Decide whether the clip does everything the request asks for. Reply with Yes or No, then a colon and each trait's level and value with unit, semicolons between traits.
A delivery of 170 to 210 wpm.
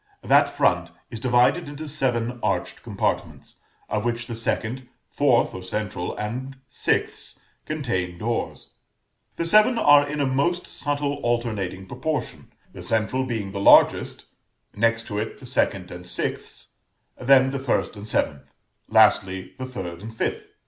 No: average, 145 wpm